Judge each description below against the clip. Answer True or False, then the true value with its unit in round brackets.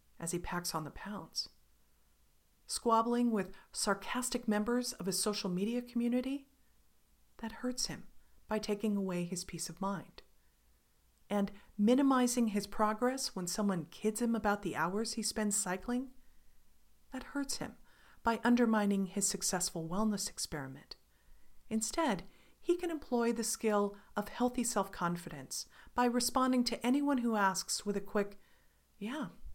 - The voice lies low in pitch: False (210 Hz)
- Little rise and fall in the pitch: False (4.1 semitones)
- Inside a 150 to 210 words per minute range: False (140 wpm)